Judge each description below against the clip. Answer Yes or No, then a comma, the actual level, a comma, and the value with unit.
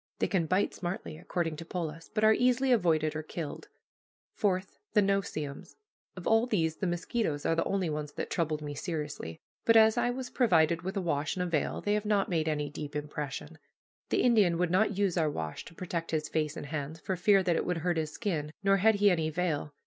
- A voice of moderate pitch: Yes, medium, 170 Hz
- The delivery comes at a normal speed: No, fast, 225 wpm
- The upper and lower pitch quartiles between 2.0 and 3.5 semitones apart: No, average, 4.3 semitones